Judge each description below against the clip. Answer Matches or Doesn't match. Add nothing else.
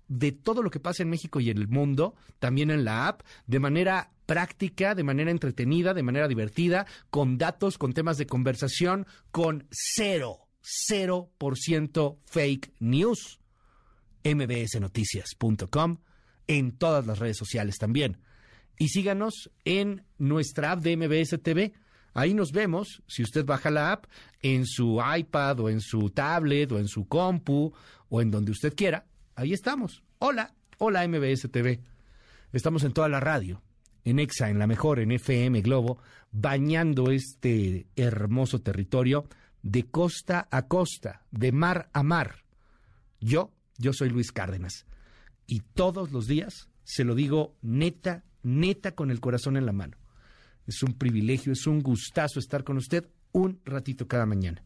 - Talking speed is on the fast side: Doesn't match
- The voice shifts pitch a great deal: Matches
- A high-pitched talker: Doesn't match